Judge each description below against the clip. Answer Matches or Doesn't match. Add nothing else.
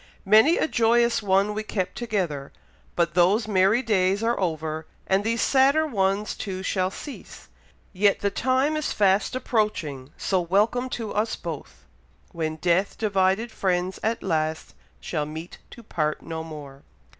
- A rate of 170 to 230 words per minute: Doesn't match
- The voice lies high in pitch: Matches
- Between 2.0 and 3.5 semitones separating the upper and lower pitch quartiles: Doesn't match